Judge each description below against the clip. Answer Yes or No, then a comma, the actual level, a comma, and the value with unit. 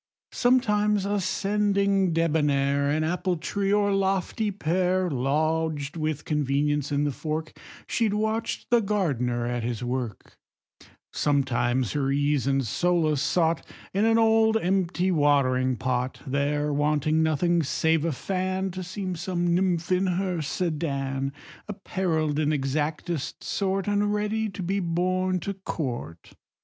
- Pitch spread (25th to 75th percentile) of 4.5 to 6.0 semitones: Yes, average, 5.1 semitones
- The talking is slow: Yes, slow, 130 wpm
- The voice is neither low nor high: Yes, medium, 165 Hz